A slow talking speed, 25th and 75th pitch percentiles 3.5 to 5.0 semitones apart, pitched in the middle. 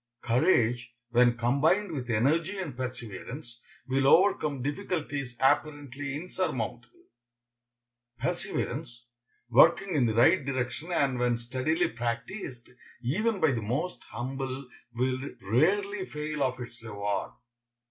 No: slow, 110 wpm; average, 4.6 semitones; low, 130 Hz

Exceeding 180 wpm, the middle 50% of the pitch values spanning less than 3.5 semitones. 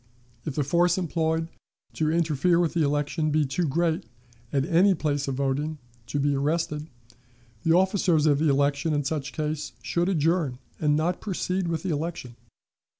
No: average, 160 wpm; average, 2.8 semitones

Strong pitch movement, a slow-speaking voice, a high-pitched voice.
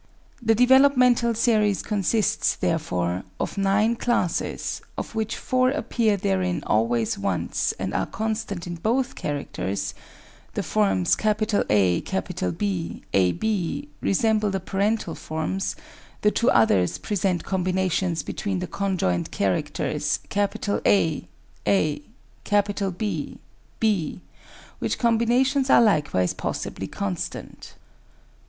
Yes: wide, 7.0 semitones; slow, 100 wpm; high, 195 Hz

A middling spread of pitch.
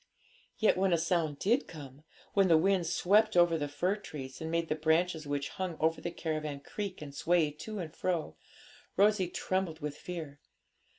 Yes: average, 3.5 semitones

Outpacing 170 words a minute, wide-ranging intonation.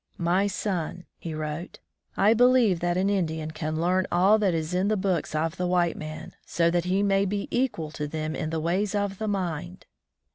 No: fast, 205 wpm; average, 3.6 semitones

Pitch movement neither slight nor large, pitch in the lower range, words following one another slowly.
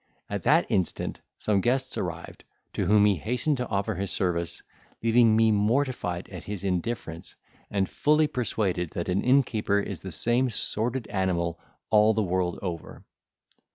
No: average, 4.6 semitones; low, 105 Hz; average, 155 wpm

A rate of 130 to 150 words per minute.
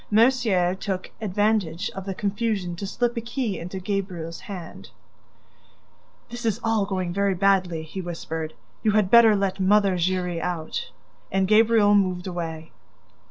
Yes: average, 145 wpm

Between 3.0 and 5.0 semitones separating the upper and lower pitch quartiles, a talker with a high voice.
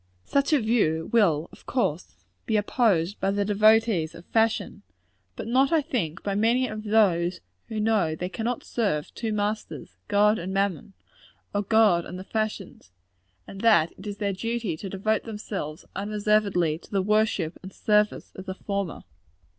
Yes: average, 3.4 semitones; high, 205 Hz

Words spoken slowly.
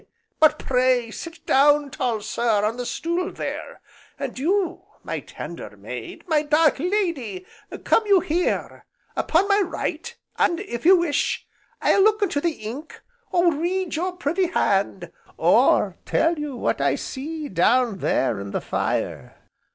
No: average, 150 wpm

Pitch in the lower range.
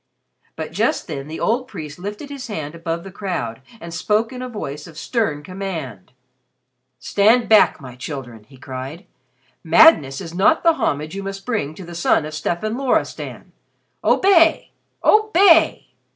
No: medium, 175 Hz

